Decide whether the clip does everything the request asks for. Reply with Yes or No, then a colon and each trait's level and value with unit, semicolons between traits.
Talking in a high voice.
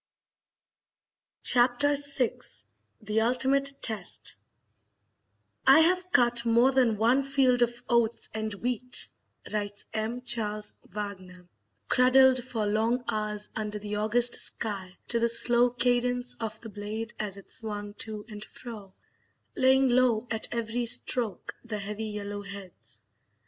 Yes: high, 230 Hz